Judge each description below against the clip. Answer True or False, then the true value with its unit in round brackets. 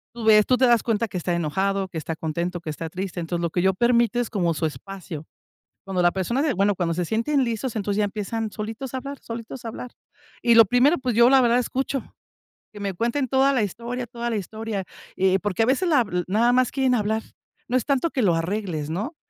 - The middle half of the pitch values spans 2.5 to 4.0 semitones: False (4.7 semitones)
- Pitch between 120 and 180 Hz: False (220 Hz)